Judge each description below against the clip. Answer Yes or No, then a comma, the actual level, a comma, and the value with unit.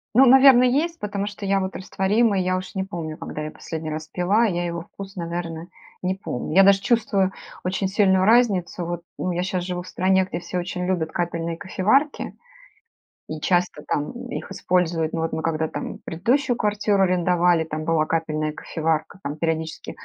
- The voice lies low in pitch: No, medium, 180 Hz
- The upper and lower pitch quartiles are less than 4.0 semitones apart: Yes, average, 3.2 semitones